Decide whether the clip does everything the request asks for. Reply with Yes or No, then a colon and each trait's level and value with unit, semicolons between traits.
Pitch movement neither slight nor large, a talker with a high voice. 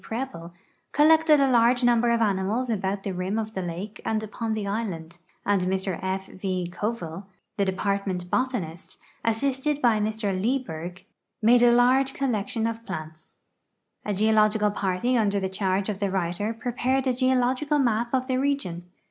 Yes: average, 4.5 semitones; high, 215 Hz